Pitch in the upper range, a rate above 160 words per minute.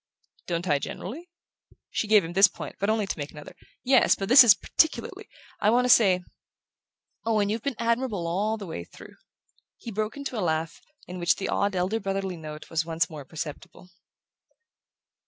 Yes: high, 195 Hz; average, 170 wpm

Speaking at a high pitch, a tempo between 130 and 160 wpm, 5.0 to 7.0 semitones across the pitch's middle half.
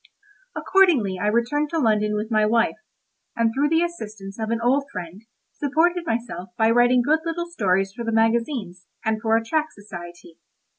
No: high, 230 Hz; average, 170 wpm; wide, 5.5 semitones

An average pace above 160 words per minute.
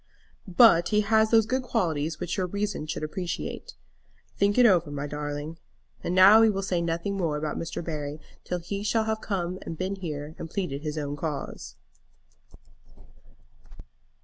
No: average, 155 wpm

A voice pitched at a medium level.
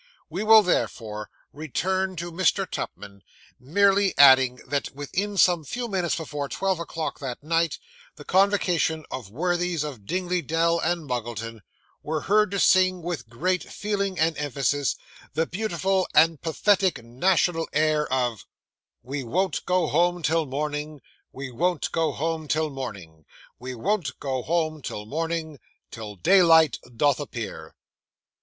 Yes: medium, 160 Hz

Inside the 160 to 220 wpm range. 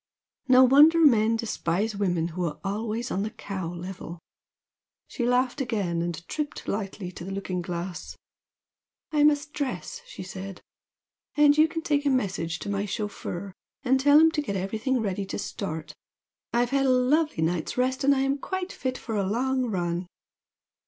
Yes: average, 170 wpm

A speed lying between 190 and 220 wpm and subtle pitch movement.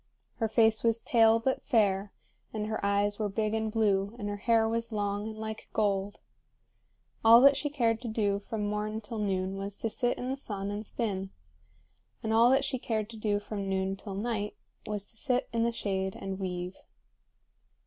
Yes: average, 195 wpm; narrow, 2.2 semitones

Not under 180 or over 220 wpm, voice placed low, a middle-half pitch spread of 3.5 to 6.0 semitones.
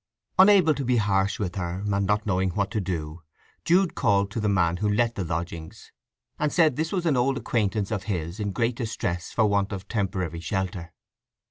Yes: average, 190 wpm; low, 100 Hz; average, 4.4 semitones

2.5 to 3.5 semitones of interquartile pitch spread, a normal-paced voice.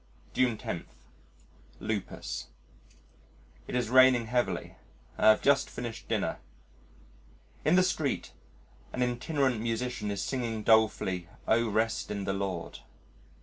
No: average, 2.8 semitones; slow, 115 wpm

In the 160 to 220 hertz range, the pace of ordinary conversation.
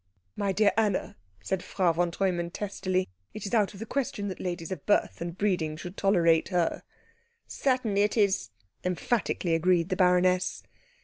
Yes: medium, 185 Hz; average, 165 wpm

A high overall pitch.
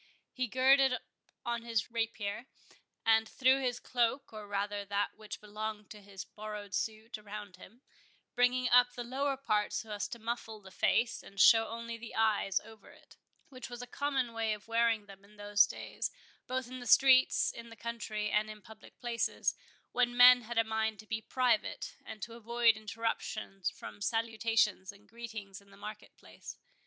Yes: high, 225 Hz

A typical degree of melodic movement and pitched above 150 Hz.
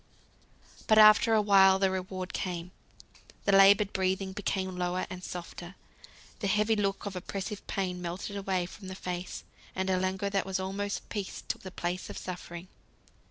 No: narrow, 1.5 semitones; high, 190 Hz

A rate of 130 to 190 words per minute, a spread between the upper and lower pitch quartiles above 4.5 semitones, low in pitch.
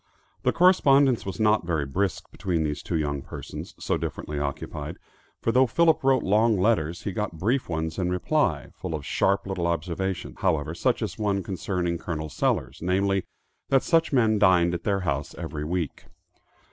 Yes: average, 170 wpm; average, 4.9 semitones; very low, 90 Hz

